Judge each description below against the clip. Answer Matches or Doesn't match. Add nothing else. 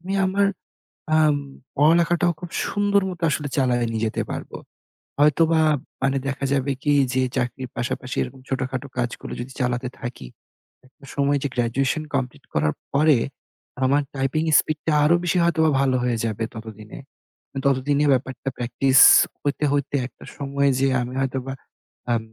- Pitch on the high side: Doesn't match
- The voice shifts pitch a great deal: Doesn't match